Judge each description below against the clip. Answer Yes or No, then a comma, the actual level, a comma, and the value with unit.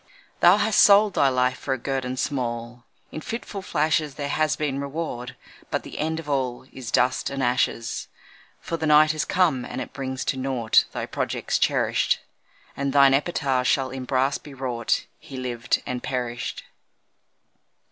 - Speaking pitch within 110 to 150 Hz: Yes, low, 135 Hz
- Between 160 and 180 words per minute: Yes, average, 165 wpm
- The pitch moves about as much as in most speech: Yes, average, 3.2 semitones